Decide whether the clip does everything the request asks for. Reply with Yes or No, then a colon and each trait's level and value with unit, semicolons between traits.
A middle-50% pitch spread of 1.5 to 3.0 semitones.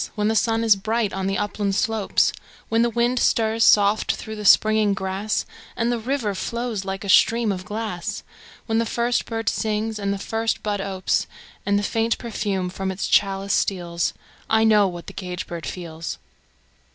Yes: average, 2.7 semitones